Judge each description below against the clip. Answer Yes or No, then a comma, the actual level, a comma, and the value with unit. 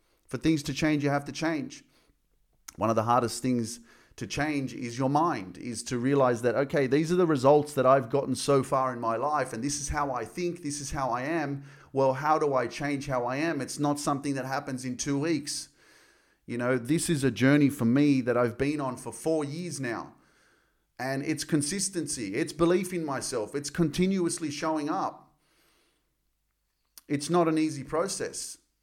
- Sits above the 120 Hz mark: Yes, medium, 140 Hz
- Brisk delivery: No, average, 195 wpm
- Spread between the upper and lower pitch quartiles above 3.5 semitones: No, average, 3.2 semitones